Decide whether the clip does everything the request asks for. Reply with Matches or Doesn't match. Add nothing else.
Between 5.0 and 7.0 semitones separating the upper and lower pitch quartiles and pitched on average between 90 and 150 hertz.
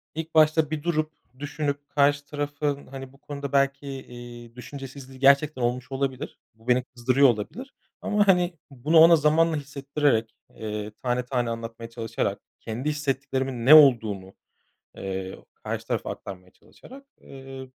Doesn't match